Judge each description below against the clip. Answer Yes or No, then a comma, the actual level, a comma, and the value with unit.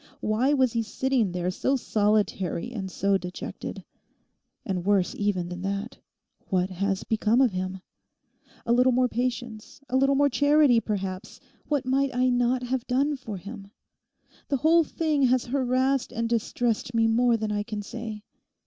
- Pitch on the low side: No, high, 235 Hz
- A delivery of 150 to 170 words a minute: Yes, average, 160 wpm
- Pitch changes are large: No, average, 4.2 semitones